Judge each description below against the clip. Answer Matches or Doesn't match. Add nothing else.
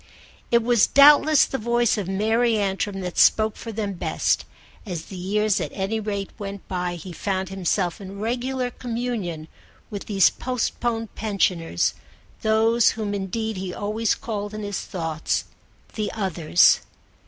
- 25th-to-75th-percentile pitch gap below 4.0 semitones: Matches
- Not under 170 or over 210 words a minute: Doesn't match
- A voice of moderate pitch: Doesn't match